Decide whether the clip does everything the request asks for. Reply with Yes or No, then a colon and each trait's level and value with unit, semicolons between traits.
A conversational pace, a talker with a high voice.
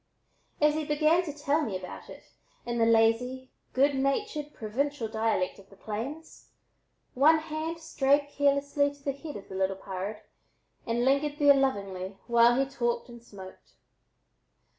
Yes: average, 155 wpm; very high, 270 Hz